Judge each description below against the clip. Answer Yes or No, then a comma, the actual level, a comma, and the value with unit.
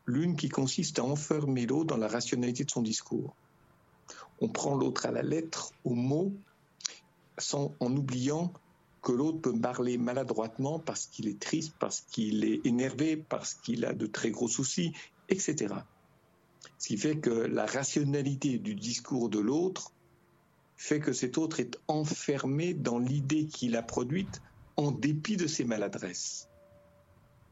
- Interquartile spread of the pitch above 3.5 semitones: Yes, average, 4.2 semitones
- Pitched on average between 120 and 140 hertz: Yes, low, 135 Hz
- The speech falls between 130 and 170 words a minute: Yes, average, 155 wpm